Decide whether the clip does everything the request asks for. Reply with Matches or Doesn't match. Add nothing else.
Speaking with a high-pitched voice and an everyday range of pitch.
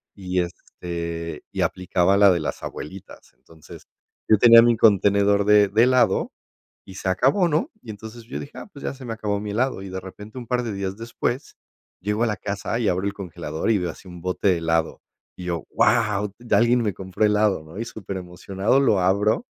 Doesn't match